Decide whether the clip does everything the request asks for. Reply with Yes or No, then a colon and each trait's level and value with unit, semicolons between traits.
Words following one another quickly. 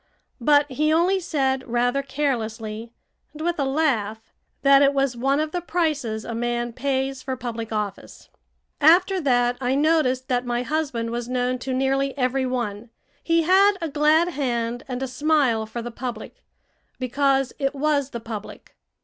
No: average, 165 wpm